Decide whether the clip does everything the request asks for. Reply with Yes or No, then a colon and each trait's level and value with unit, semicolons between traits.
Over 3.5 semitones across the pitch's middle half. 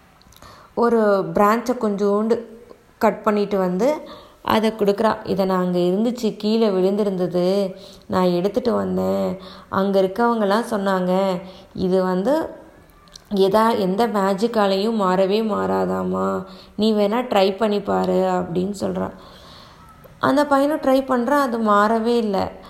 No: average, 3.2 semitones